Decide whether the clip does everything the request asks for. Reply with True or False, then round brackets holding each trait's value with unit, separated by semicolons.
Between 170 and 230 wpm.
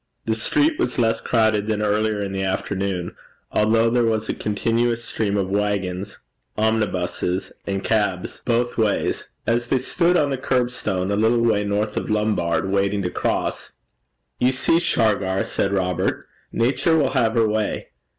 False (160 wpm)